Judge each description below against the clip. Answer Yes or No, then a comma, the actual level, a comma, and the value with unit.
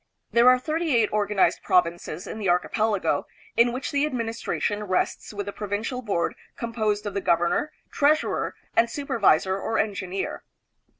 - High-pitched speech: Yes, high, 215 Hz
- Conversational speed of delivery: Yes, average, 155 wpm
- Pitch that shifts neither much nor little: Yes, average, 3.5 semitones